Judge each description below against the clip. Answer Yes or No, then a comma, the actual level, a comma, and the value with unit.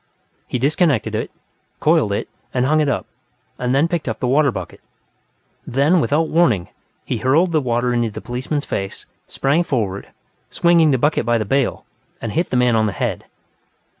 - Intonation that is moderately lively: Yes, average, 4.6 semitones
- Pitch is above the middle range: No, low, 135 Hz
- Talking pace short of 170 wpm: No, average, 180 wpm